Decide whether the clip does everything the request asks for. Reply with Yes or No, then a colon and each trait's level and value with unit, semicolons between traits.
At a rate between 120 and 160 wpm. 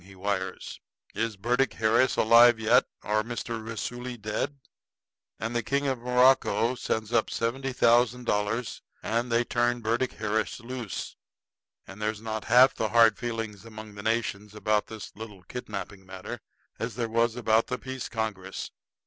Yes: average, 155 wpm